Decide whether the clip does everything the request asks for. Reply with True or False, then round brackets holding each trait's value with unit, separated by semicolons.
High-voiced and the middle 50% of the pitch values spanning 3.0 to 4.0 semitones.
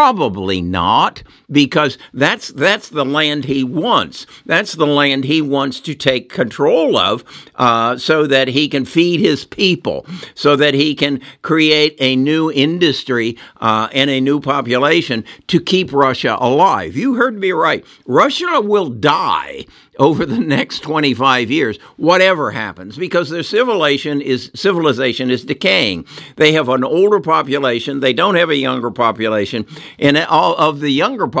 False (145 Hz; 3.4 semitones)